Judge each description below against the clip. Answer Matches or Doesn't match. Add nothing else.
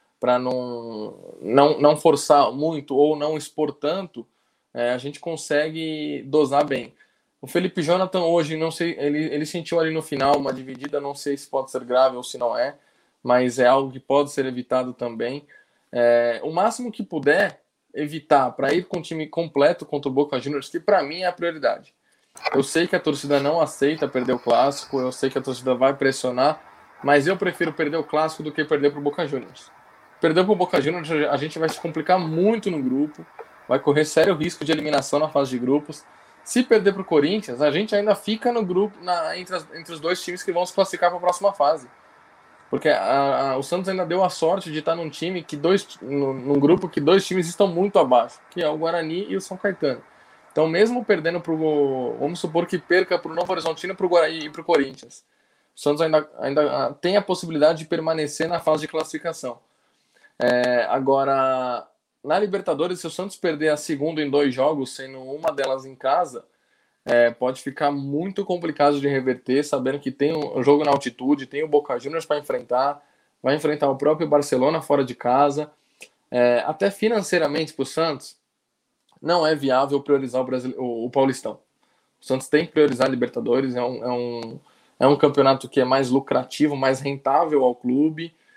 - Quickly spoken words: Matches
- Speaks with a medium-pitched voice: Matches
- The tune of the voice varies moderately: Matches